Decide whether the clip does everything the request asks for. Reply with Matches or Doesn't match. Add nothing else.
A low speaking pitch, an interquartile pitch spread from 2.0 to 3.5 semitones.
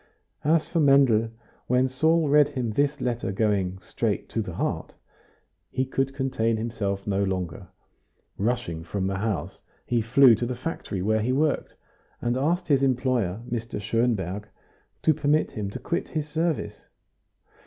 Doesn't match